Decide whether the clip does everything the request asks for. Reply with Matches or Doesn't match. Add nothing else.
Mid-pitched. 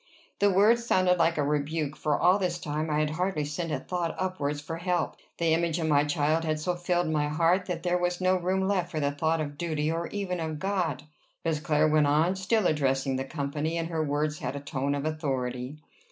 Matches